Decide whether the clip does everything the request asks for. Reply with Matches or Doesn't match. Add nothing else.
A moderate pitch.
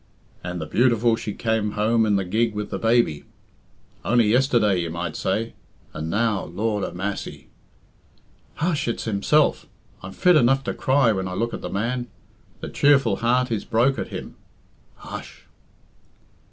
Doesn't match